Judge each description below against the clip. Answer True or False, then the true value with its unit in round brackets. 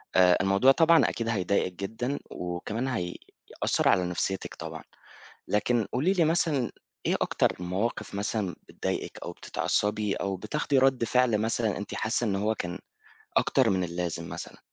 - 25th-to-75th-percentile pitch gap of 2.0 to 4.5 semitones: False (4.9 semitones)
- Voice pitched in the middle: False (105 Hz)